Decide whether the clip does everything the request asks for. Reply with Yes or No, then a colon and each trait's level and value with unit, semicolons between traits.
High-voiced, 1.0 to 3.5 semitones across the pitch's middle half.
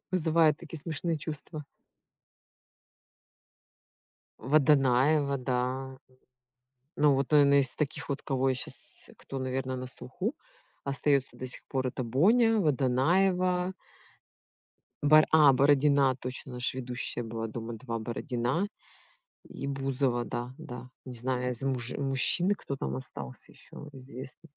No: low, 135 Hz; average, 3.2 semitones